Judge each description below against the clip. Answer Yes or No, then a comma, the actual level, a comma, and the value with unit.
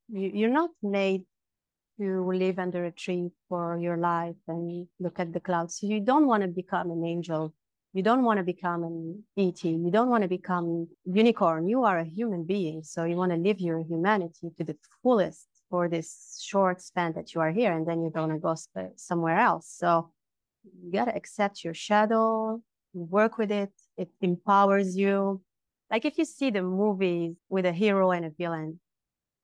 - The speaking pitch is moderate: Yes, medium, 180 Hz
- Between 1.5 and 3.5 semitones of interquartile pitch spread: Yes, average, 3.2 semitones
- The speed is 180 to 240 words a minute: Yes, average, 185 wpm